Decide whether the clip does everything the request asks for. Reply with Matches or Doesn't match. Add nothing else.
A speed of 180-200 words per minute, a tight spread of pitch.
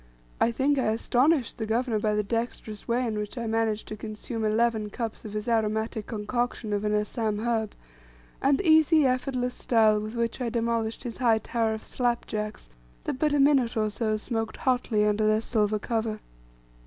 Matches